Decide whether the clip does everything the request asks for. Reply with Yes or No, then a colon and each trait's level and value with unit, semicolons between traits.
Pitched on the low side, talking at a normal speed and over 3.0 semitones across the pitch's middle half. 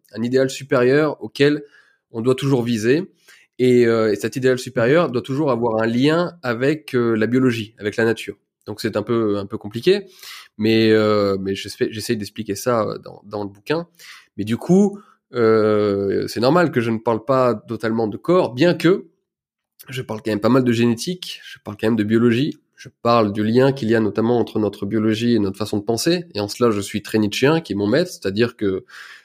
Yes: low, 115 Hz; average, 210 wpm; average, 3.7 semitones